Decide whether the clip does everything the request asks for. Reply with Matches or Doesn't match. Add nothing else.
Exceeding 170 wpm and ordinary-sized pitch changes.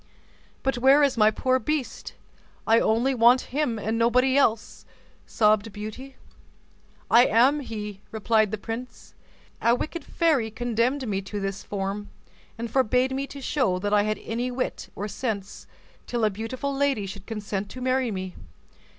Doesn't match